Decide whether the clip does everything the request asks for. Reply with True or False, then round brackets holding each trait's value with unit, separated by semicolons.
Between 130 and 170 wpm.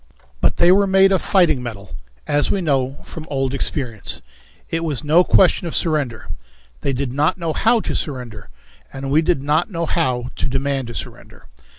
False (185 wpm)